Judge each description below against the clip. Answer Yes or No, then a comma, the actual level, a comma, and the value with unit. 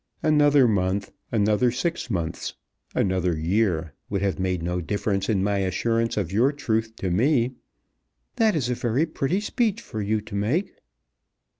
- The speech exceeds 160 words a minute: No, average, 155 wpm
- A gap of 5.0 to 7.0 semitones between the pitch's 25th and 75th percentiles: Yes, wide, 5.6 semitones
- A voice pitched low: Yes, low, 110 Hz